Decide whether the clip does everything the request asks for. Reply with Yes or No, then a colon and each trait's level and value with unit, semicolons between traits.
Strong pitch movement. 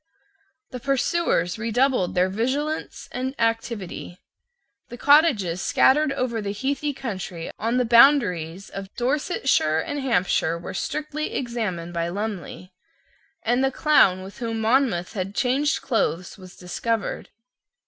Yes: wide, 6.4 semitones